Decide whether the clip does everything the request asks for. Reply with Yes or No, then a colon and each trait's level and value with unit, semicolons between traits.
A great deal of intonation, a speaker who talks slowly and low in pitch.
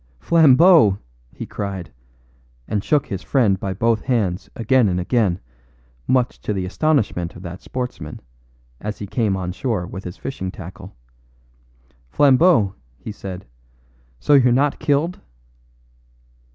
Yes: wide, 5.9 semitones; slow, 130 wpm; low, 105 Hz